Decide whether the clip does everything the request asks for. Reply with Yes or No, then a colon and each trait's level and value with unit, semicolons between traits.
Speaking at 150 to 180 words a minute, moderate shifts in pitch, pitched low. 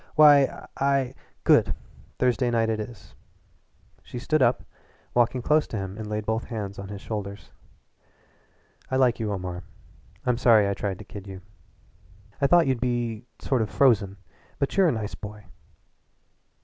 Yes: average, 160 wpm; average, 3.9 semitones; low, 115 Hz